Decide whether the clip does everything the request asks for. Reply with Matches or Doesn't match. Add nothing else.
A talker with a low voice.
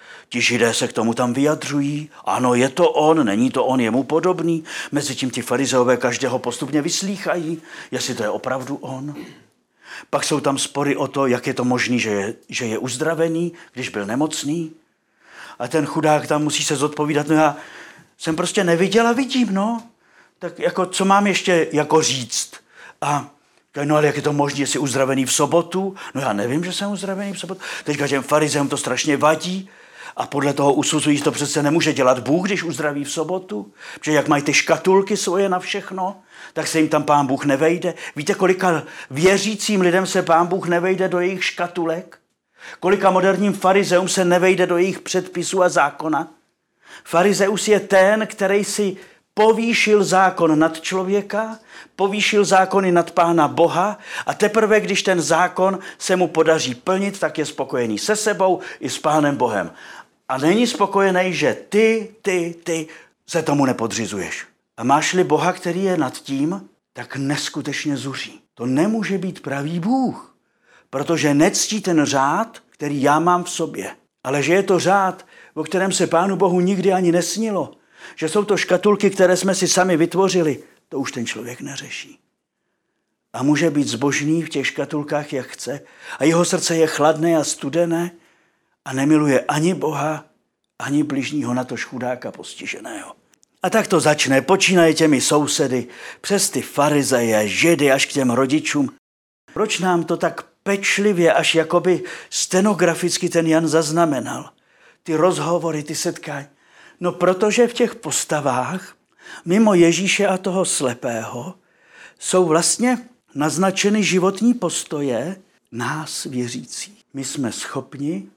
Doesn't match